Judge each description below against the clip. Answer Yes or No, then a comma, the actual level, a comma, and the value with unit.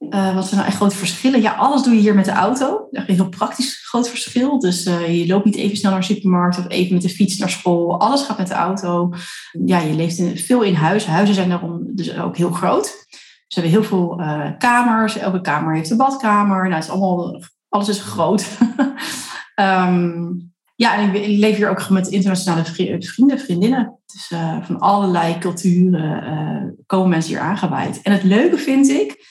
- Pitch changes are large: No, average, 3.2 semitones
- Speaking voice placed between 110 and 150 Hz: No, high, 190 Hz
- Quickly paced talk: Yes, fast, 210 wpm